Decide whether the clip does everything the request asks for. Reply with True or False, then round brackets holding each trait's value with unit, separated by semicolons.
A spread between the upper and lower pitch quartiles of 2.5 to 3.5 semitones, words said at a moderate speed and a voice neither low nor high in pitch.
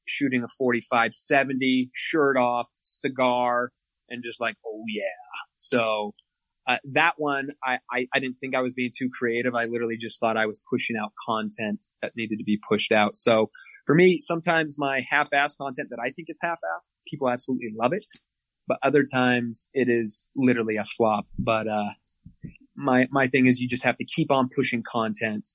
False (3.0 semitones; 185 wpm; 125 Hz)